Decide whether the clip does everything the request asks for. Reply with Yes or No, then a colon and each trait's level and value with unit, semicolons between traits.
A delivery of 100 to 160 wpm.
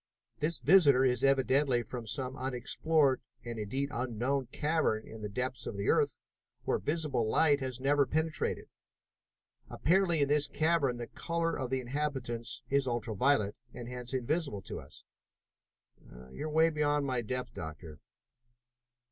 Yes: average, 145 wpm